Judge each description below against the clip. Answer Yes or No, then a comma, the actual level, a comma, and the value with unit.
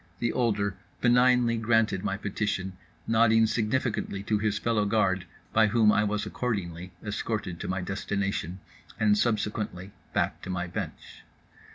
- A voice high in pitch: No, low, 105 Hz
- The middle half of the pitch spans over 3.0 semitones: No, average, 2.7 semitones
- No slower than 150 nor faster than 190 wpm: No, average, 140 wpm